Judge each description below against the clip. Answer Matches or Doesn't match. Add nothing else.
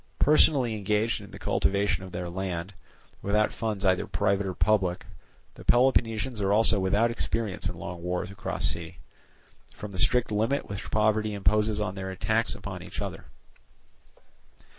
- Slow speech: Doesn't match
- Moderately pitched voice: Doesn't match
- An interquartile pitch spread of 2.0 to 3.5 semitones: Matches